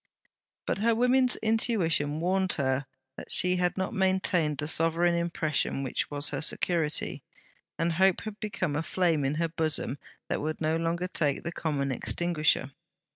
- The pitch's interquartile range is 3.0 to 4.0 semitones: Yes, average, 3.7 semitones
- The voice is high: No, medium, 165 Hz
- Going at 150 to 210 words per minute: Yes, average, 160 wpm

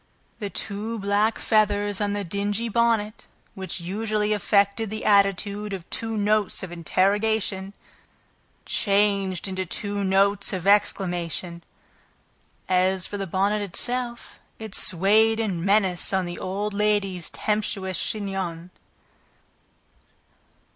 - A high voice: Yes, high, 200 Hz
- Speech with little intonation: Yes, narrow, 1.9 semitones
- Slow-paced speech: Yes, slow, 115 wpm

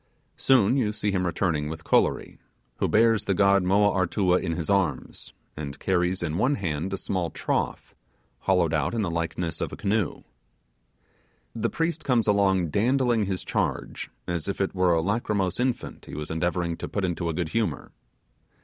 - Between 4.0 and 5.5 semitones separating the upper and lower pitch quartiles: No, average, 3.6 semitones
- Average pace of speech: Yes, average, 175 wpm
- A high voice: No, very low, 95 Hz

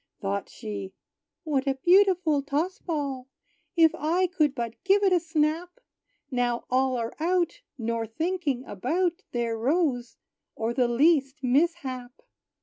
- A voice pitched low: No, very high, 280 Hz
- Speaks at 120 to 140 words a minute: Yes, slow, 135 wpm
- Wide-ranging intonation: Yes, wide, 5.9 semitones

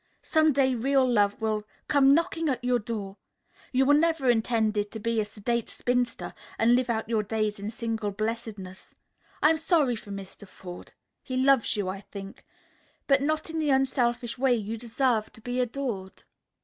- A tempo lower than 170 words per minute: No, average, 175 wpm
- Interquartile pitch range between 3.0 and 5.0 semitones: Yes, average, 3.9 semitones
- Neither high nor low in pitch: No, high, 235 Hz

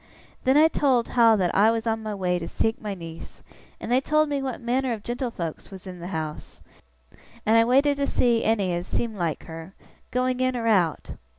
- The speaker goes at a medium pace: No, fast, 210 wpm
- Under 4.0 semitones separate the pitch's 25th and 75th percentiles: No, wide, 5.6 semitones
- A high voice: Yes, high, 225 Hz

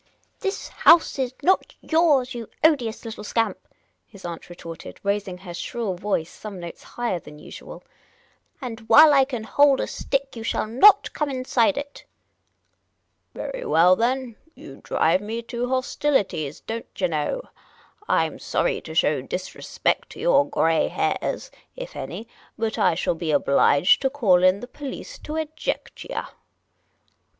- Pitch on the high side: Yes, high, 235 Hz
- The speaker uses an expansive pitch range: Yes, wide, 7.4 semitones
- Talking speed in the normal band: Yes, average, 165 wpm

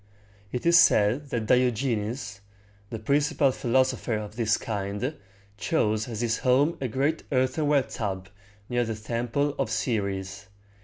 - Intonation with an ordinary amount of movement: Yes, average, 3.7 semitones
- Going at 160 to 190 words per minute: No, slow, 135 wpm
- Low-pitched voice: Yes, low, 120 Hz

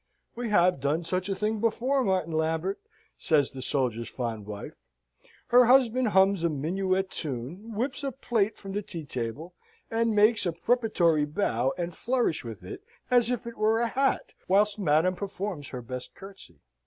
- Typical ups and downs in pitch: No, wide, 6.8 semitones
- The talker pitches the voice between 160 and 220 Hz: Yes, high, 190 Hz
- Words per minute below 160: No, average, 170 wpm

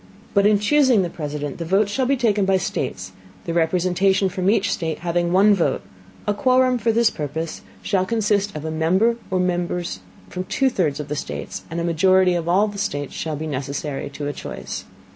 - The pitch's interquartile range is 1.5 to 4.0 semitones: No, average, 4.4 semitones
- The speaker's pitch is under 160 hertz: No, medium, 185 Hz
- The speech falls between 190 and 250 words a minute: Yes, average, 200 wpm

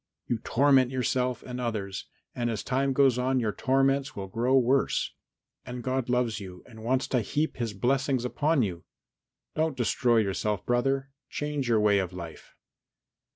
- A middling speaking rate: Yes, average, 160 wpm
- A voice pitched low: Yes, low, 125 Hz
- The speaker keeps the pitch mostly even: No, average, 3.4 semitones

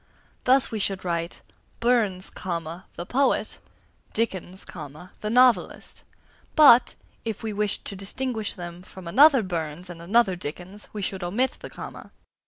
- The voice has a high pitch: Yes, high, 195 Hz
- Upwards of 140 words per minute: No, slow, 135 wpm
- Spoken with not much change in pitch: No, average, 4.8 semitones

